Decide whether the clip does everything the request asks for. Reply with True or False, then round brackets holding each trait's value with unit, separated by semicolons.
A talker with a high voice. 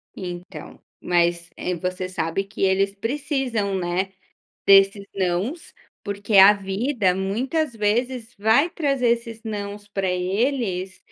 True (200 Hz)